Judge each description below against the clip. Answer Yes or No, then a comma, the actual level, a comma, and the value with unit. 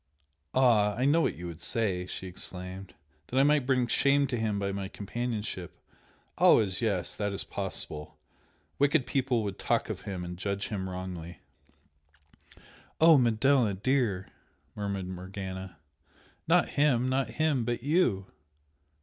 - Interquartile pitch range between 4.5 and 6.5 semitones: Yes, wide, 5.5 semitones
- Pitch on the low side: Yes, low, 105 Hz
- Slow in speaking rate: No, average, 145 wpm